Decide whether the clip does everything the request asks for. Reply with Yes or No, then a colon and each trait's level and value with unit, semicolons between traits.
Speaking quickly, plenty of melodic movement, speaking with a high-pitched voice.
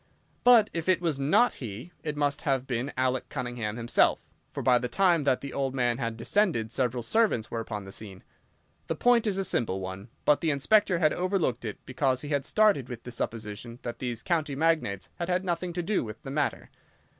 No: fast, 210 wpm; wide, 6.3 semitones; low, 135 Hz